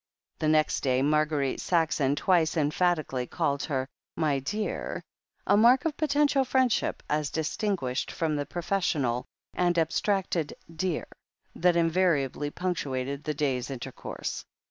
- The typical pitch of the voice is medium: Yes, medium, 155 Hz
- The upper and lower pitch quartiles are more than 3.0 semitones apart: Yes, average, 4.5 semitones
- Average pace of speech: No, slow, 130 wpm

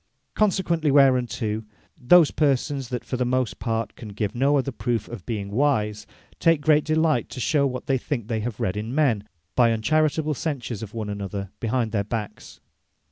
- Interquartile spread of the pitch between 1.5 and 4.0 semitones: No, average, 4.9 semitones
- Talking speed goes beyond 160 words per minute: Yes, average, 180 wpm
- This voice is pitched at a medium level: No, low, 125 Hz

